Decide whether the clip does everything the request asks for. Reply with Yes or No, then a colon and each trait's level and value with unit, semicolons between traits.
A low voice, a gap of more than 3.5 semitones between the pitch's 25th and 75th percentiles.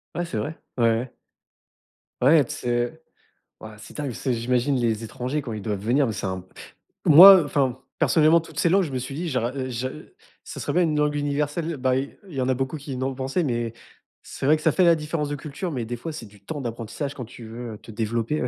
Yes: low, 130 Hz; average, 4.2 semitones